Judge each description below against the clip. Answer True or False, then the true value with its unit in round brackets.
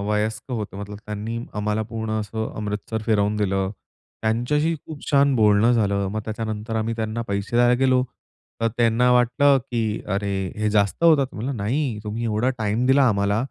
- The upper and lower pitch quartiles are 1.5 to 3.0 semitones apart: True (2.7 semitones)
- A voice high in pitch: False (110 Hz)